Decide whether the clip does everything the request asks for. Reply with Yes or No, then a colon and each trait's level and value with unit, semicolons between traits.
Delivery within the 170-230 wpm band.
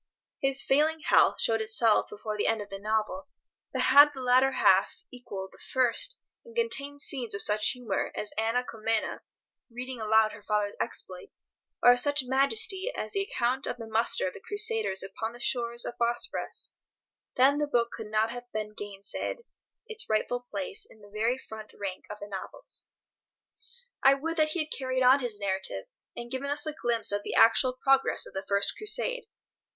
Yes: average, 190 wpm